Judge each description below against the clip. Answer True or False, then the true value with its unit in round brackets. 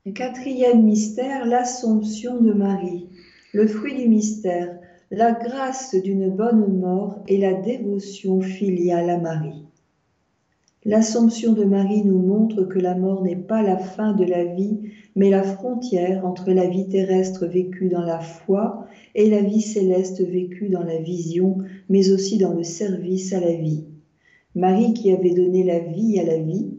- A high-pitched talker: True (195 Hz)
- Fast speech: False (160 wpm)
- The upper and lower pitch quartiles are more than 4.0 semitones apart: False (2.8 semitones)